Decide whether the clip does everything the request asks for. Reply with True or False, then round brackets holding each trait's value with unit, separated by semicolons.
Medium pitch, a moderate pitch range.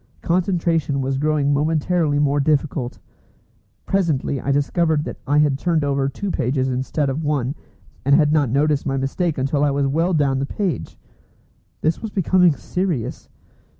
True (145 Hz; 3.0 semitones)